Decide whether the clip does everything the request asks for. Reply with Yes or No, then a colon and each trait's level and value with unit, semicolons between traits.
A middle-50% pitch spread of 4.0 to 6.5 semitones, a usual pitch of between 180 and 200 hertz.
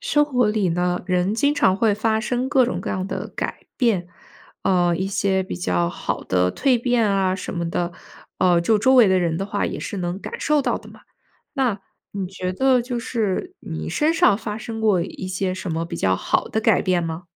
Yes: average, 4.8 semitones; high, 195 Hz